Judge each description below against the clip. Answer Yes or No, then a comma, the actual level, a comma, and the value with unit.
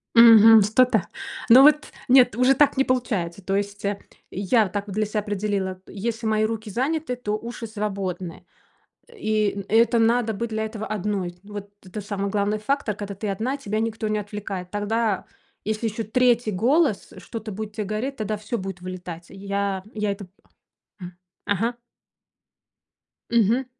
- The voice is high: Yes, high, 215 Hz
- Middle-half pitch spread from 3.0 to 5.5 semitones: No, narrow, 2.5 semitones